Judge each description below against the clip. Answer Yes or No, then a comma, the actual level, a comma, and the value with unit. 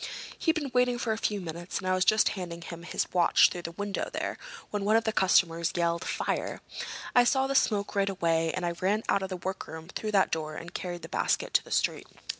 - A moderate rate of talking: No, fast, 235 wpm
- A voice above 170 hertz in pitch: Yes, medium, 185 Hz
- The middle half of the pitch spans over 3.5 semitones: Yes, average, 3.9 semitones